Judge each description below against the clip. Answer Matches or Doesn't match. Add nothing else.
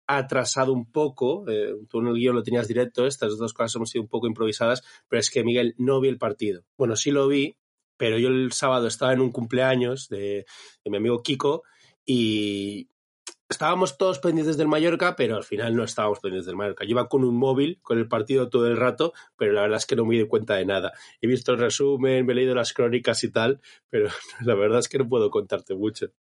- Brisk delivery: Matches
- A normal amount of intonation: Matches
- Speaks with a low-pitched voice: Matches